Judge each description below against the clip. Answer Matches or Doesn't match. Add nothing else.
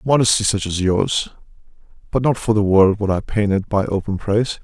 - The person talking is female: Doesn't match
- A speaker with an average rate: Matches